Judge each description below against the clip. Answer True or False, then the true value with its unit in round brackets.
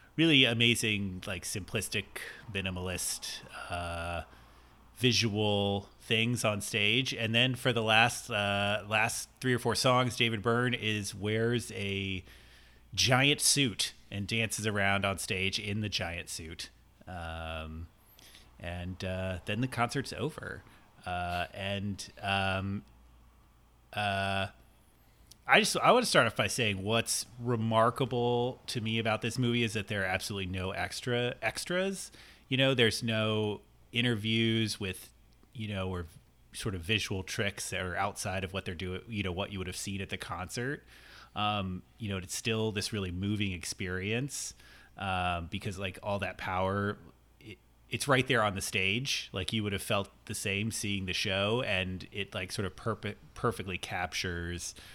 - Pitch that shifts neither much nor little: True (3.5 semitones)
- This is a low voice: True (100 Hz)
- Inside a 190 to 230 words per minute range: False (155 wpm)